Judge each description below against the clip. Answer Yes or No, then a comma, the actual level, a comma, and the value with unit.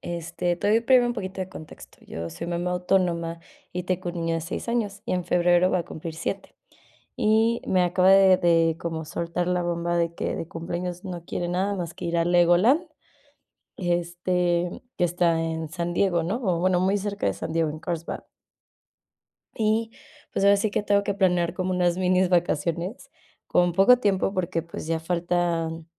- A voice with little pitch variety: Yes, narrow, 2.0 semitones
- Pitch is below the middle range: No, medium, 175 Hz